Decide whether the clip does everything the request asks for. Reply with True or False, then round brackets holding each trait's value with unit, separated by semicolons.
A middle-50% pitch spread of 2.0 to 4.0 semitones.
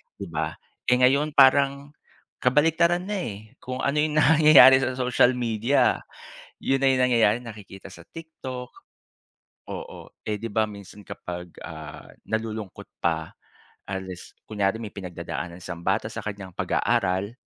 False (5.6 semitones)